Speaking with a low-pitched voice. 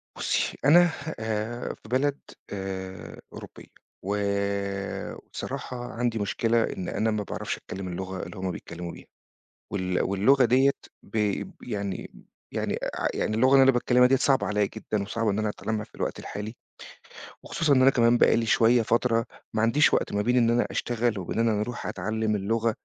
Yes: low, 110 Hz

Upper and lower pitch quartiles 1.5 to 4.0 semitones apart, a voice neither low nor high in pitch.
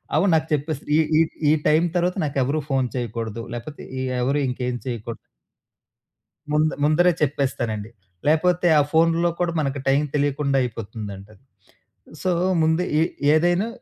No: average, 4.4 semitones; medium, 145 Hz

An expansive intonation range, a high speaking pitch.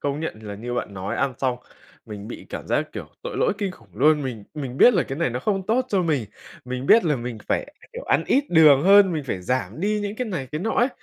No: wide, 7.9 semitones; medium, 145 Hz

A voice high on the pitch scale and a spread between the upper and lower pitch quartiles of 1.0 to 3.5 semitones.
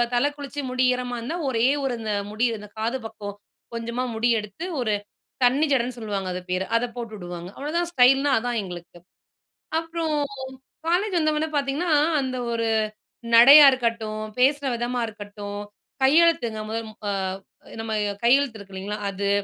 No: high, 240 Hz; average, 4.6 semitones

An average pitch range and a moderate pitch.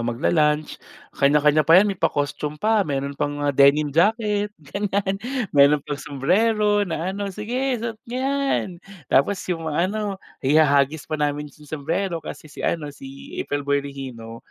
No: wide, 6.0 semitones; medium, 155 Hz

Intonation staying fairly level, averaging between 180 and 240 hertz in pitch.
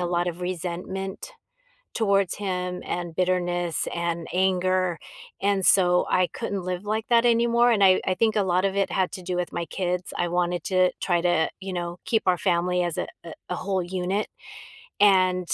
Yes: narrow, 1.7 semitones; medium, 185 Hz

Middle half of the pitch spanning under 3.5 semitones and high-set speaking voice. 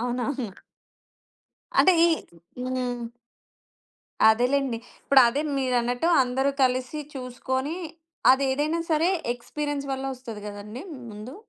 Yes: narrow, 2.4 semitones; very high, 255 Hz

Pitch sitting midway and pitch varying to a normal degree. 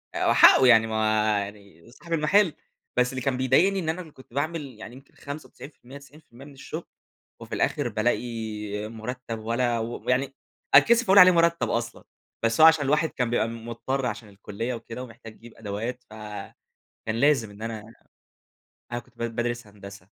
No: low, 120 Hz; average, 3.9 semitones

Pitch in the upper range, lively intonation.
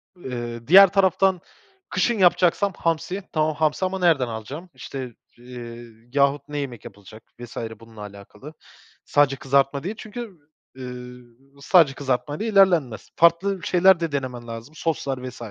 No: medium, 140 Hz; wide, 6.3 semitones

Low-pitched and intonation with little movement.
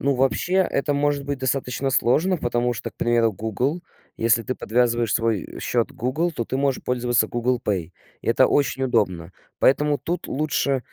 No: low, 125 Hz; average, 3.2 semitones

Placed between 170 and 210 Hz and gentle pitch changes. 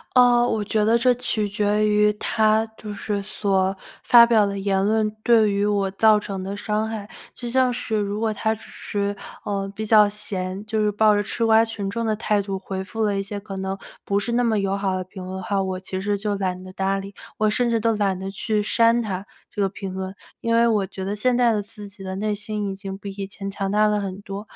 Yes: high, 205 Hz; narrow, 1.9 semitones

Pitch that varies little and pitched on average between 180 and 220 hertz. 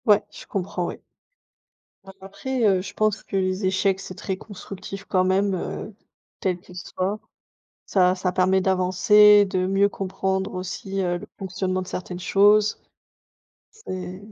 Yes: narrow, 1.4 semitones; high, 190 Hz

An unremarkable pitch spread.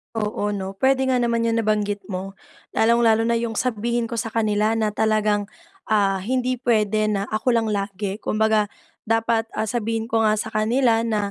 No: narrow, 1.7 semitones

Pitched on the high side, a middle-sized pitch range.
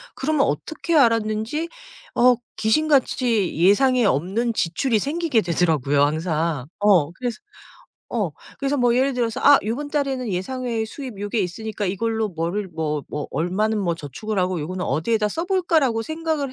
No: high, 220 Hz; wide, 6.6 semitones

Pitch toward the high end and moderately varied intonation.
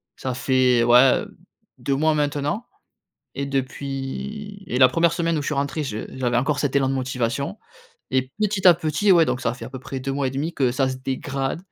No: low, 135 Hz; average, 3.3 semitones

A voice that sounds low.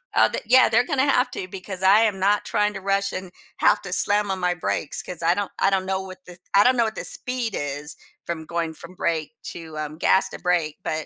No: medium, 185 Hz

